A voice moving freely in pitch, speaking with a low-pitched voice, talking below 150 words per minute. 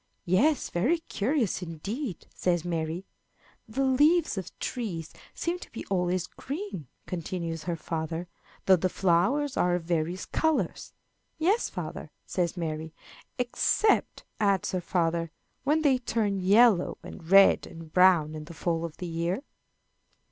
No: wide, 6.7 semitones; medium, 185 Hz; average, 140 wpm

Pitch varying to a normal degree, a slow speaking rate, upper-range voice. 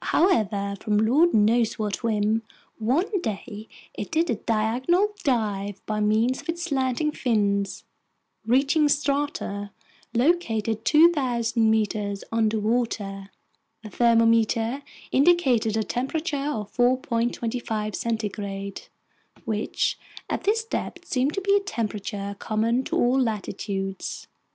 Yes: average, 4.5 semitones; slow, 115 wpm; high, 230 Hz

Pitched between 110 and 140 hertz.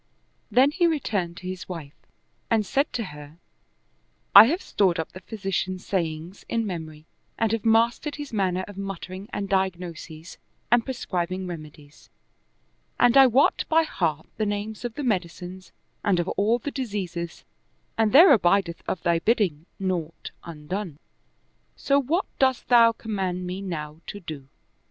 No: high, 190 Hz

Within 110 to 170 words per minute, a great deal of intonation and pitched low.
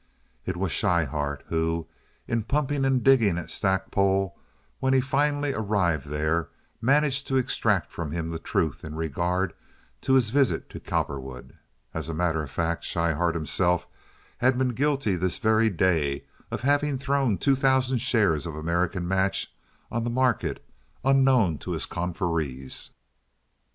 Yes: average, 145 wpm; wide, 8.1 semitones; very low, 95 Hz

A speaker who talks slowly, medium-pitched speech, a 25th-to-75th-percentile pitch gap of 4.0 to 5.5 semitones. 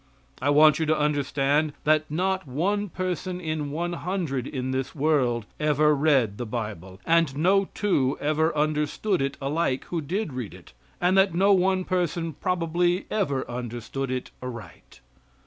No: average, 155 wpm; medium, 155 Hz; average, 4.7 semitones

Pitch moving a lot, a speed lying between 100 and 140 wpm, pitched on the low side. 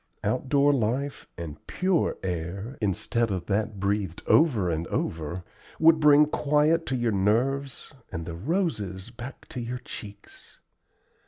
Yes: wide, 6.8 semitones; slow, 135 wpm; low, 115 Hz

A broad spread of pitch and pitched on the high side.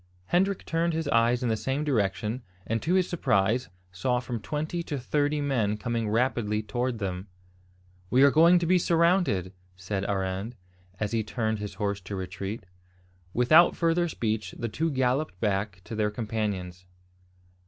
No: wide, 6.3 semitones; low, 115 Hz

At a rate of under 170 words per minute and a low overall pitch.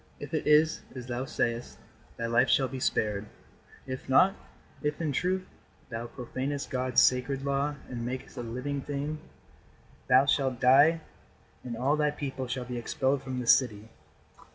Yes: average, 160 wpm; low, 130 Hz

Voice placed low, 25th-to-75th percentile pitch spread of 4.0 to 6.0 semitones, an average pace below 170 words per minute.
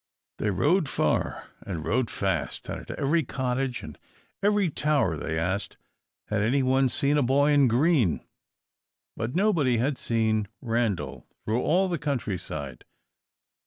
Yes: low, 125 Hz; wide, 5.5 semitones; average, 140 wpm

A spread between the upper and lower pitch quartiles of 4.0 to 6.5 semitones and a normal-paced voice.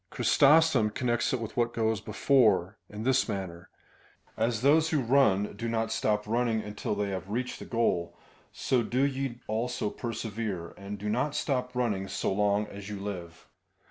No: average, 3.5 semitones; average, 170 wpm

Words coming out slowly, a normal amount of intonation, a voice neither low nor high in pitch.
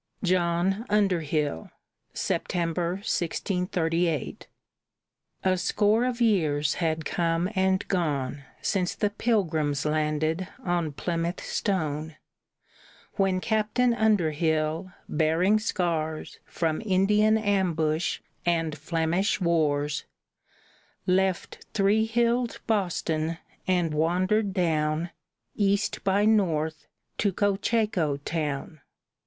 Yes: slow, 90 wpm; average, 4.1 semitones; medium, 175 Hz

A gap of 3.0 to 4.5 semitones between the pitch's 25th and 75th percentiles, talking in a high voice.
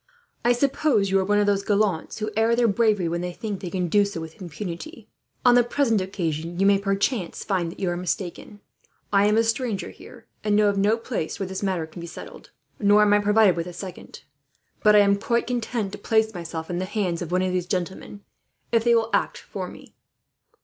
Yes: average, 3.4 semitones; high, 200 Hz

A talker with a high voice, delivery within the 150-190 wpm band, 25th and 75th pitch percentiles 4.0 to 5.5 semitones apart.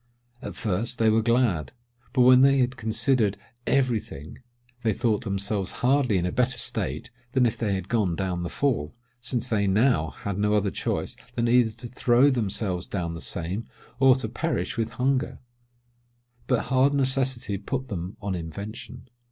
No: low, 115 Hz; average, 170 wpm; average, 4.5 semitones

